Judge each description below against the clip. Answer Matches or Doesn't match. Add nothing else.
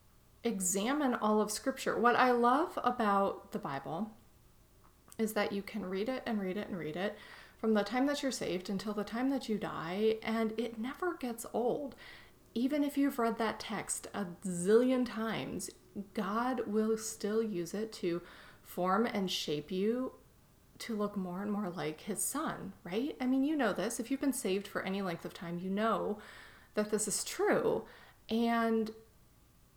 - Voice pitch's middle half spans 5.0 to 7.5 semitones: Doesn't match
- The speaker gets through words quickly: Doesn't match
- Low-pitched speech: Doesn't match